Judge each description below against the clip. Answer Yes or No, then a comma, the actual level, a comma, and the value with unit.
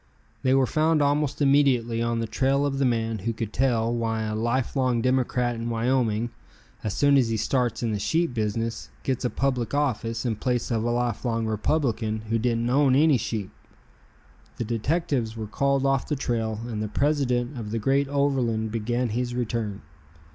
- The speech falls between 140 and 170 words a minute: No, average, 185 wpm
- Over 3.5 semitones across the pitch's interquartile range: No, average, 3.1 semitones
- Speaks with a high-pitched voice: No, low, 120 Hz